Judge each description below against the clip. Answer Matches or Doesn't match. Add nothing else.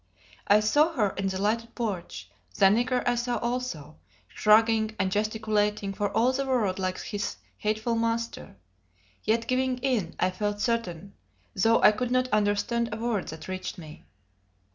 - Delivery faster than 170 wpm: Doesn't match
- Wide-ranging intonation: Doesn't match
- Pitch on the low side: Doesn't match